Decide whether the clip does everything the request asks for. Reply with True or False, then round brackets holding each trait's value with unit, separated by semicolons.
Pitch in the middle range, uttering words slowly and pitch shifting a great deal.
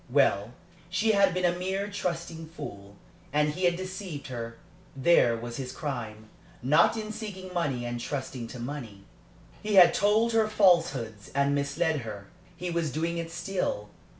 False (160 Hz; 160 wpm; 7.1 semitones)